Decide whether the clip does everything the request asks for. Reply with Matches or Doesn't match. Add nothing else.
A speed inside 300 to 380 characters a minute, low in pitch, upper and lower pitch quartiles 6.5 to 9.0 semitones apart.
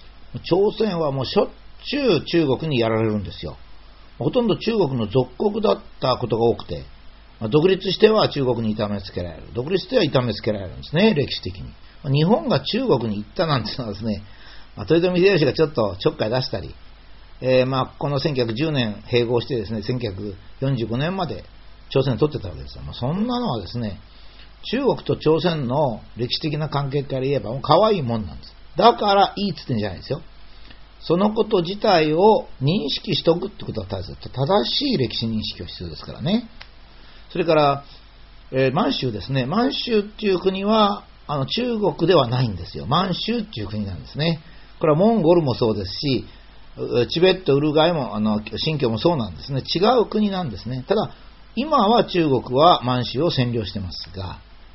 Matches